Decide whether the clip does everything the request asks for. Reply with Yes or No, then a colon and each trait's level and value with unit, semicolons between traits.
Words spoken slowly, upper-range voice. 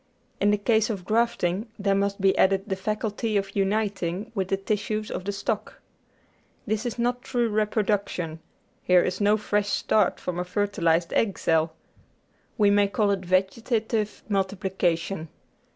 No: average, 155 wpm; high, 200 Hz